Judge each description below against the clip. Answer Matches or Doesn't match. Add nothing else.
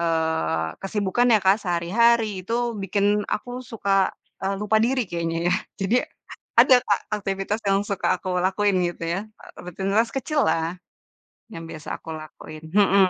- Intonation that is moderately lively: Matches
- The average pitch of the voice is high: Matches